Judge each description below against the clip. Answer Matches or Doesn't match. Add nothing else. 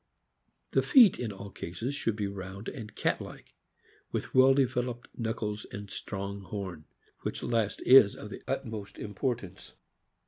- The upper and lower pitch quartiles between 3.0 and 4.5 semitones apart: Matches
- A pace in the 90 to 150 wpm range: Matches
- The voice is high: Doesn't match